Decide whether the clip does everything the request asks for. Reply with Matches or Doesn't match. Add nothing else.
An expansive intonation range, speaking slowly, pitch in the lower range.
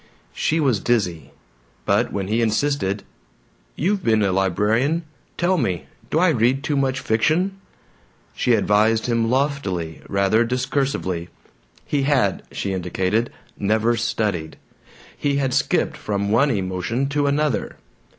Matches